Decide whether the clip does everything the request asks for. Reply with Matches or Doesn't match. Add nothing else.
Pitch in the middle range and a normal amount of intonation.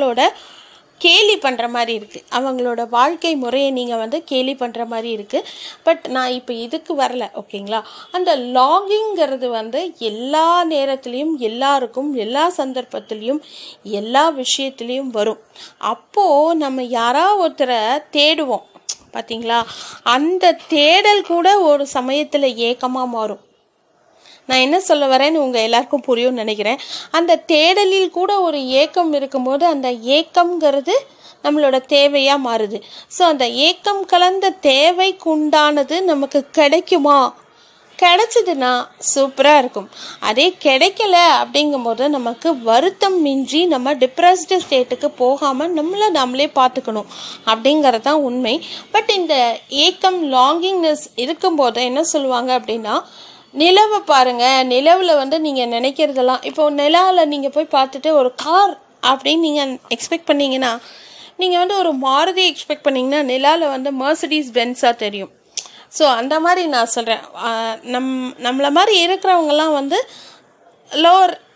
Doesn't match